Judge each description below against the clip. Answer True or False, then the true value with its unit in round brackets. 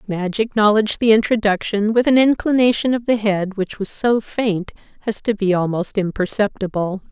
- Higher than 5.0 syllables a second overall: True (5.2 syllables/s)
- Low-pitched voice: False (210 Hz)